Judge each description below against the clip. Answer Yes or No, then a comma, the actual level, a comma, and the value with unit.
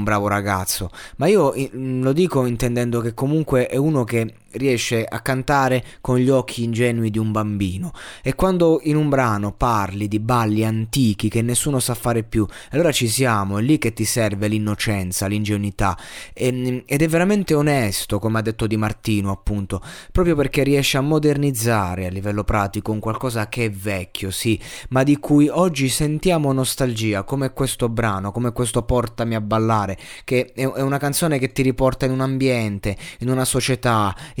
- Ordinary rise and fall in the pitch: Yes, average, 4.0 semitones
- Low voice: Yes, low, 120 Hz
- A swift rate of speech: Yes, fast, 175 wpm